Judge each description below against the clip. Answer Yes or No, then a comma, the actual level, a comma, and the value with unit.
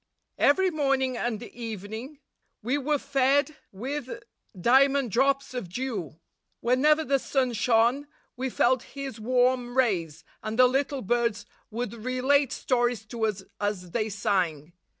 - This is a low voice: No, high, 245 Hz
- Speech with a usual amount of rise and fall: Yes, average, 3.9 semitones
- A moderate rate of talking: No, slow, 130 wpm